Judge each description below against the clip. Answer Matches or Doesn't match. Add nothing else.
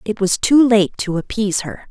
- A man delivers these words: Doesn't match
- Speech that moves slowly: Doesn't match